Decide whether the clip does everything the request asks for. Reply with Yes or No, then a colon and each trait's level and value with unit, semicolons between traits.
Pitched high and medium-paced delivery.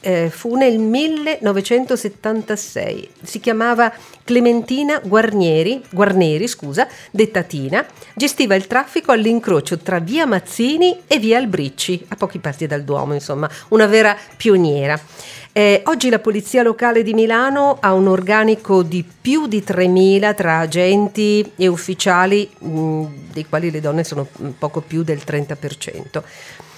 Yes: high, 205 Hz; average, 130 wpm